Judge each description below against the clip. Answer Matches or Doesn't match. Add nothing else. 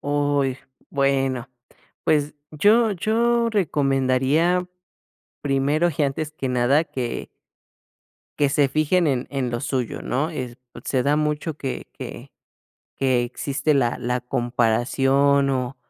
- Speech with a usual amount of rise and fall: Matches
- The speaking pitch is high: Doesn't match